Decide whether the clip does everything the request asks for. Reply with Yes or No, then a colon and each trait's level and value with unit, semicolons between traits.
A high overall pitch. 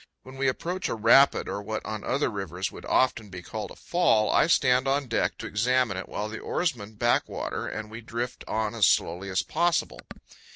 No: low, 115 Hz